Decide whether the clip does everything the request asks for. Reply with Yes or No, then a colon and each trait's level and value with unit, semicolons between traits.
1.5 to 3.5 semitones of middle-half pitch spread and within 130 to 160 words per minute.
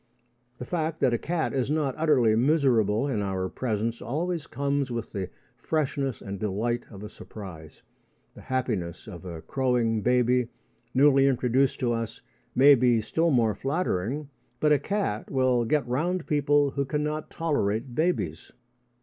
No: average, 4.8 semitones; average, 150 wpm